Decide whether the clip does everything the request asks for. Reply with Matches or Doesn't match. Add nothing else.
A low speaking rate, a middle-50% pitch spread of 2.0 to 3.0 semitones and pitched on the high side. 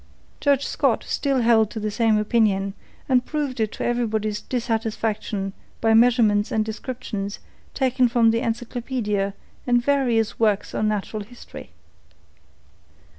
Matches